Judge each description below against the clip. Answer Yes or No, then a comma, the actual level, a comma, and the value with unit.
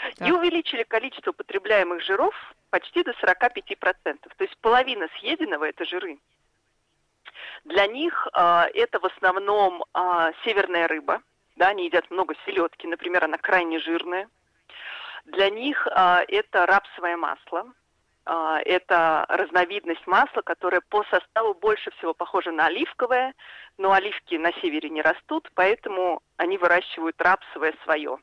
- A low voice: No, high, 190 Hz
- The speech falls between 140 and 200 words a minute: No, average, 130 wpm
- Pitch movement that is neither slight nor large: No, wide, 6.9 semitones